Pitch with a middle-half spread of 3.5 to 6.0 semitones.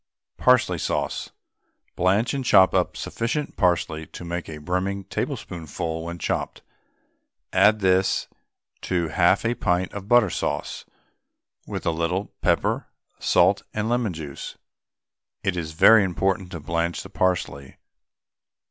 No: average, 3.0 semitones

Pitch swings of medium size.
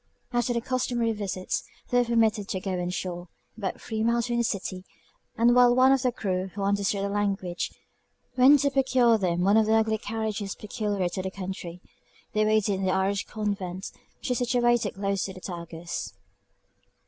Yes: average, 3.9 semitones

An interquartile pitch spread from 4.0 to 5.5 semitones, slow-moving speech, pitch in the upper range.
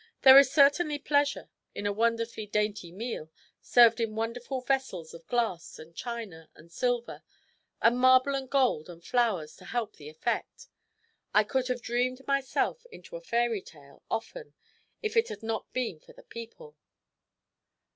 No: average, 4.3 semitones; average, 155 wpm; high, 235 Hz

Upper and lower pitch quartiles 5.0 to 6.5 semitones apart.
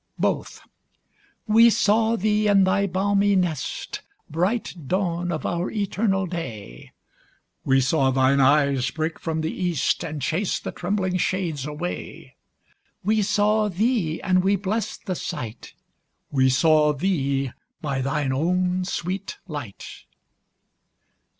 Yes: wide, 5.5 semitones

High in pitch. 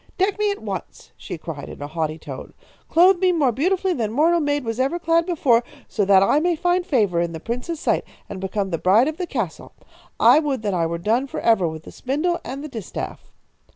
Yes: very high, 255 Hz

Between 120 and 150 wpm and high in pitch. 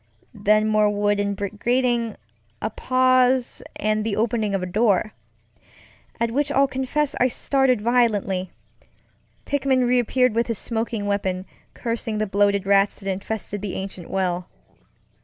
Yes: average, 140 wpm; high, 215 Hz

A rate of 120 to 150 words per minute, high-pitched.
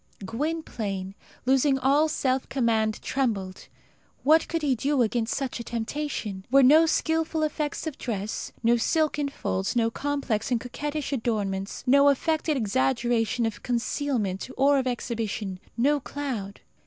Yes: average, 140 wpm; very high, 255 Hz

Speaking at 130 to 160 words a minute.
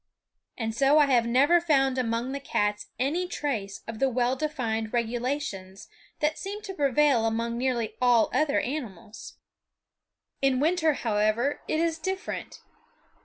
Yes: average, 140 wpm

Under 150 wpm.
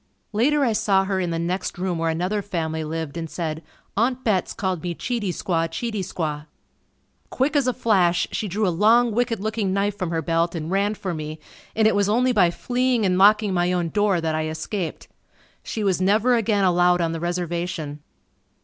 No: average, 200 wpm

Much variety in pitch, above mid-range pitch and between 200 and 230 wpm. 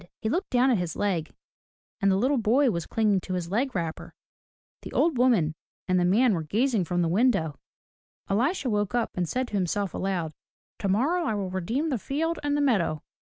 Yes: wide, 6.1 semitones; high, 205 Hz; fast, 205 wpm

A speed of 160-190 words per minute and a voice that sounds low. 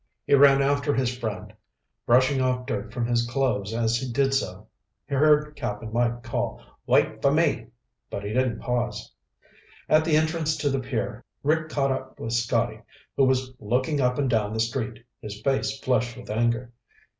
Yes: average, 180 wpm; low, 125 Hz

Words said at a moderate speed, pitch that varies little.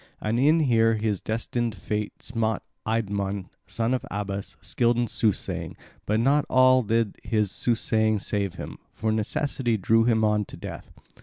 Yes: average, 155 wpm; narrow, 2.1 semitones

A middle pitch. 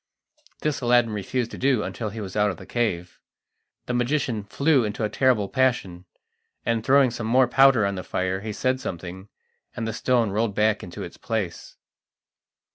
No: low, 110 Hz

